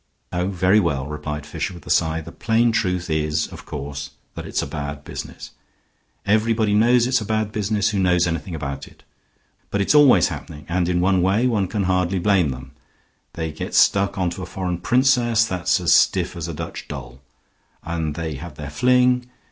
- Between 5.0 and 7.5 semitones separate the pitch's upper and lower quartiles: Yes, wide, 5.5 semitones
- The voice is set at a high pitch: No, very low, 90 Hz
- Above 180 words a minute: Yes, average, 195 wpm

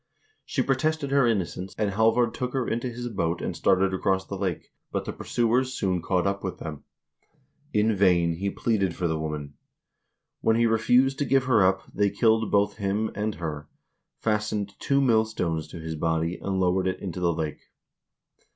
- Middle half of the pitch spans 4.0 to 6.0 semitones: Yes, average, 4.3 semitones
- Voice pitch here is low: Yes, low, 100 Hz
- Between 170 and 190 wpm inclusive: Yes, average, 185 wpm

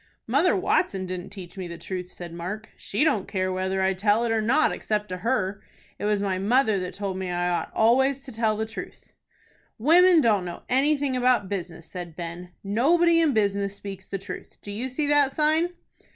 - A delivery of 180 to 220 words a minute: Yes, average, 200 wpm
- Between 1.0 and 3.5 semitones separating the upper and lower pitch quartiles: No, wide, 5.6 semitones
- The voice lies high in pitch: Yes, high, 205 Hz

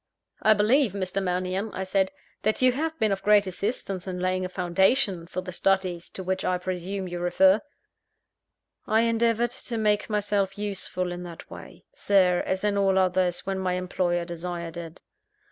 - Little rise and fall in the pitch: Yes, narrow, 2.3 semitones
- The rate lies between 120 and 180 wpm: Yes, average, 175 wpm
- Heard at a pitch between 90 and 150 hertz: No, high, 190 Hz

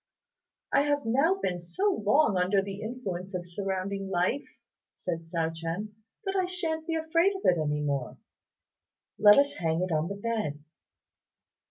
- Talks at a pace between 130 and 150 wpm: No, average, 160 wpm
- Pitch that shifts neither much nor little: No, wide, 8.6 semitones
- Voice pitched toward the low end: No, high, 200 Hz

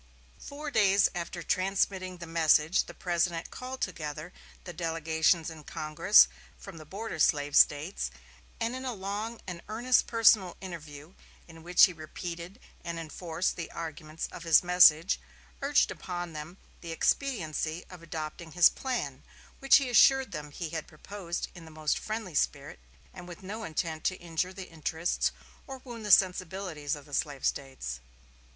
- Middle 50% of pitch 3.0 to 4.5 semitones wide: Yes, average, 3.6 semitones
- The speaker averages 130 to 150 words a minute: No, average, 160 wpm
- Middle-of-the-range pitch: Yes, medium, 170 Hz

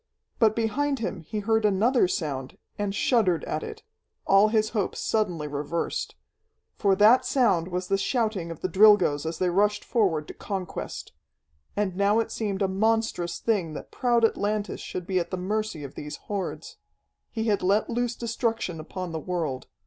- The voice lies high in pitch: Yes, high, 200 Hz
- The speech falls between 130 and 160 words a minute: No, average, 170 wpm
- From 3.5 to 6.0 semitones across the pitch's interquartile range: Yes, average, 4.0 semitones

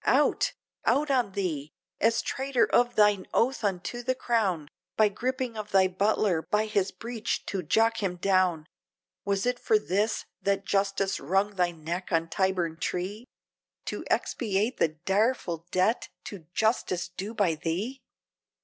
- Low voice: No, high, 200 Hz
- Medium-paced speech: Yes, average, 150 wpm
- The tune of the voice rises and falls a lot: No, average, 3.9 semitones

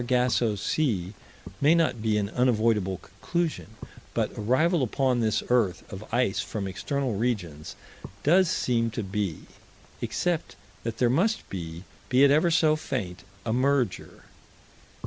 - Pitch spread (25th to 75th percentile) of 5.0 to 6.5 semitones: Yes, wide, 5.4 semitones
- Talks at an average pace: Yes, average, 145 wpm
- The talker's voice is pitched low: Yes, low, 120 Hz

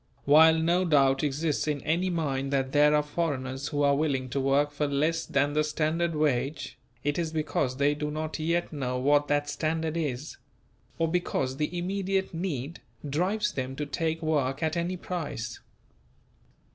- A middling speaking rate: Yes, average, 170 wpm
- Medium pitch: Yes, medium, 150 Hz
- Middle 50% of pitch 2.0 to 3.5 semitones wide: Yes, average, 2.7 semitones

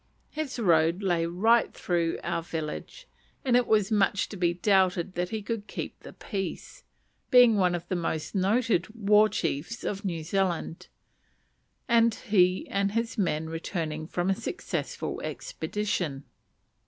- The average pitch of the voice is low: No, high, 190 Hz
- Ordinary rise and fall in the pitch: Yes, average, 4.3 semitones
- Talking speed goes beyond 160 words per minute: No, average, 145 wpm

